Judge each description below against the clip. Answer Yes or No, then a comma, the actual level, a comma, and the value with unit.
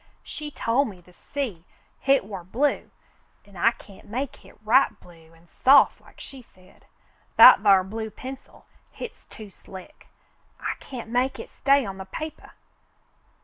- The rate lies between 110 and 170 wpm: Yes, average, 155 wpm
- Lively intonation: Yes, wide, 6.0 semitones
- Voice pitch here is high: Yes, high, 225 Hz